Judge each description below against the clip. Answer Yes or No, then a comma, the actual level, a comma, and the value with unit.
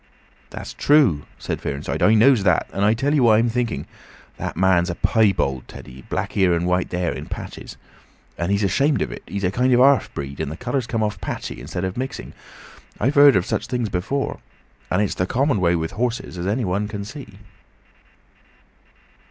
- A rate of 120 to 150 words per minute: No, average, 195 wpm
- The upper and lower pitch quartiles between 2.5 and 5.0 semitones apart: No, wide, 5.6 semitones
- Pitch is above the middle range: No, low, 105 Hz